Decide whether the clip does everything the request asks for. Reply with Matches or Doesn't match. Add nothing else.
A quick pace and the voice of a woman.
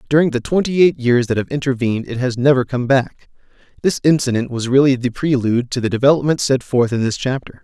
Doesn't match